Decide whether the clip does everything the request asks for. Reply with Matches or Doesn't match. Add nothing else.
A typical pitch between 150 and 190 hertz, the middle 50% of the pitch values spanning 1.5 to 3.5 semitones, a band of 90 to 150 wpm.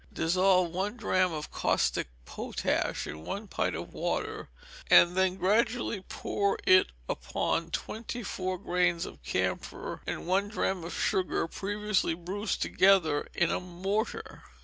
Matches